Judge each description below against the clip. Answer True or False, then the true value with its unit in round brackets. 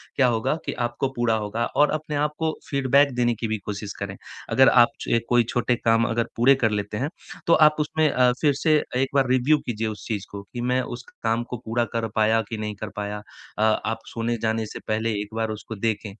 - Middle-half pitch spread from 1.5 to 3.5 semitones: True (2.9 semitones)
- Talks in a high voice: False (115 Hz)